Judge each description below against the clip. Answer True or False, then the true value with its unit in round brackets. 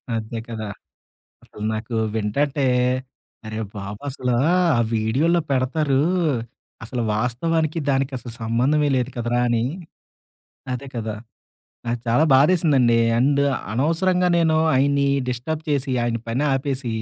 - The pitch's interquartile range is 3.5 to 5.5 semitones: True (4.0 semitones)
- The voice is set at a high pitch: False (130 Hz)